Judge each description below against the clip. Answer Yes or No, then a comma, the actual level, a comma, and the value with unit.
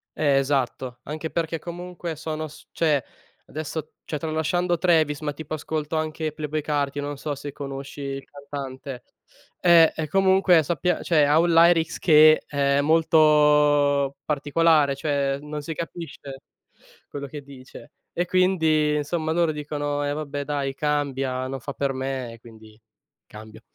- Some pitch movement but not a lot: No, narrow, 2.3 semitones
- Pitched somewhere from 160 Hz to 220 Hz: No, medium, 150 Hz